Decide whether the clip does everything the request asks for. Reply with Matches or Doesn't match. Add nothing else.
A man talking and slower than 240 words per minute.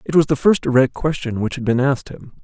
Doesn't match